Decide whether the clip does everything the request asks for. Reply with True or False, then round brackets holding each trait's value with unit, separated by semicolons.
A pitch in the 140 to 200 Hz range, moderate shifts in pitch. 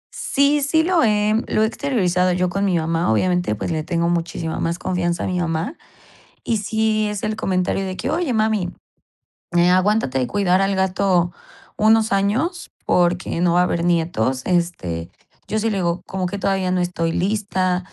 True (185 Hz; 3.7 semitones)